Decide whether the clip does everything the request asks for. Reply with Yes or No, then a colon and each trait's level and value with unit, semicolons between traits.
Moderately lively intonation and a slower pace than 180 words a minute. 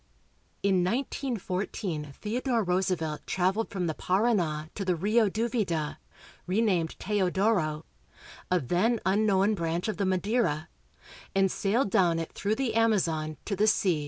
Yes: average, 4.2 semitones; slow, 135 wpm